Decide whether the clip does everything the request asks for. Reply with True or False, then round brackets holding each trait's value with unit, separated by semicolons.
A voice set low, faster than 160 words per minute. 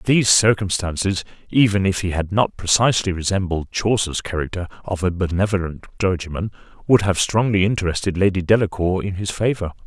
False (95 Hz; 145 wpm)